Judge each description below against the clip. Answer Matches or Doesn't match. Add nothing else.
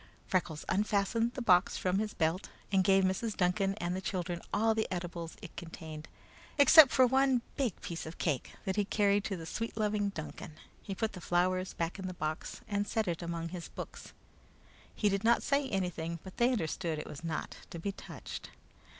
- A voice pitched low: Doesn't match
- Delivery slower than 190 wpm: Doesn't match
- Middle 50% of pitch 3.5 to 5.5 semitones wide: Matches